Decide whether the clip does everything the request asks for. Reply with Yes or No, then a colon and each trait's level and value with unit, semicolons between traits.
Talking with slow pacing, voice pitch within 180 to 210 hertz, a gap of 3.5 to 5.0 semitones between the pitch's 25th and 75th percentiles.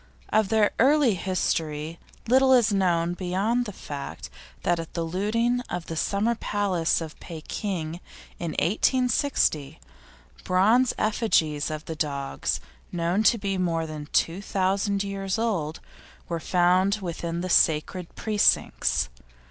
Yes: slow, 130 wpm; medium, 185 Hz; average, 4.4 semitones